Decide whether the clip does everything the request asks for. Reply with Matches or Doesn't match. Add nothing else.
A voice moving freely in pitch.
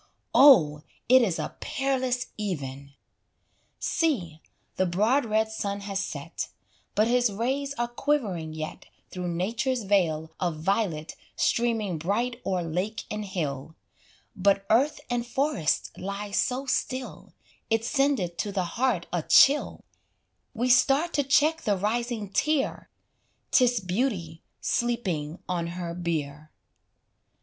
Matches